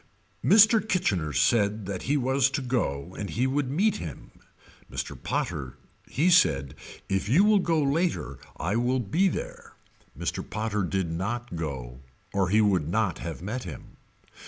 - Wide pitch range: Yes, wide, 8.5 semitones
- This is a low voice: Yes, low, 110 Hz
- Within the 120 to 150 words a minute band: No, average, 160 wpm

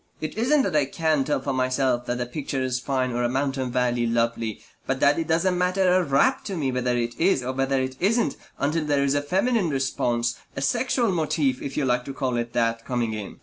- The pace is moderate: No, fast, 230 wpm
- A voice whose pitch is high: No, low, 135 Hz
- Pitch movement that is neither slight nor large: Yes, average, 4.5 semitones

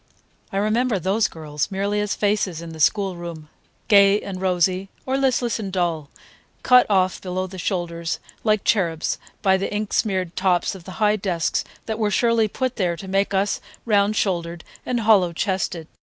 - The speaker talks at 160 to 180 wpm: Yes, average, 170 wpm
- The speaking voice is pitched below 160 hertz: No, high, 195 Hz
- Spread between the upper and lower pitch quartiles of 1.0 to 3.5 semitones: Yes, average, 3.2 semitones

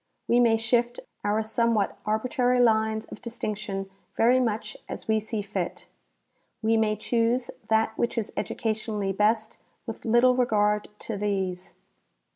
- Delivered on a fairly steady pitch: Yes, narrow, 1.9 semitones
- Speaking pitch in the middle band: No, high, 220 Hz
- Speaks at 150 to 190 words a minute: No, average, 140 wpm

